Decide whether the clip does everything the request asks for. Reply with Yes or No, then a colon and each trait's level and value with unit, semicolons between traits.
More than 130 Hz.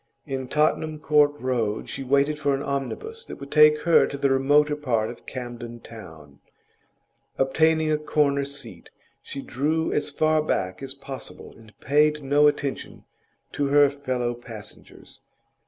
Yes: medium, 140 Hz